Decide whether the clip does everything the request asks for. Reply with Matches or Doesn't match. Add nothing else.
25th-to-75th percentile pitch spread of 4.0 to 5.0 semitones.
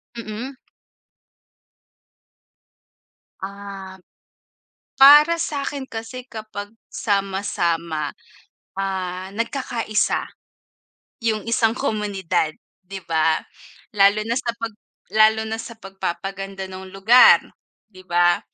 Doesn't match